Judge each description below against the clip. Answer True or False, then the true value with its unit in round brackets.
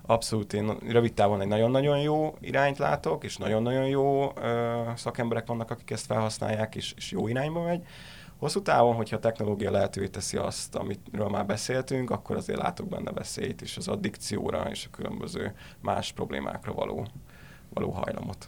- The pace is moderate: False (160 wpm)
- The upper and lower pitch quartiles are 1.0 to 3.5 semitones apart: False (3.9 semitones)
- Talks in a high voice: False (115 Hz)